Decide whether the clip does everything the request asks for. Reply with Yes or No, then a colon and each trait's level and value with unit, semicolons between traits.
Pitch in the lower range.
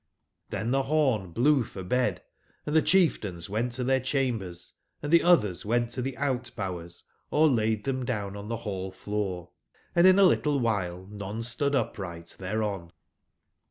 Yes: low, 115 Hz